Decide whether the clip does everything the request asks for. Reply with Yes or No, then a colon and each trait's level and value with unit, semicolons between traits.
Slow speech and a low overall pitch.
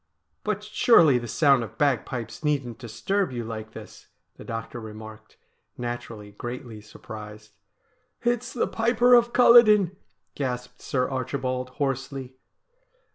Yes: slow, 130 wpm; low, 125 Hz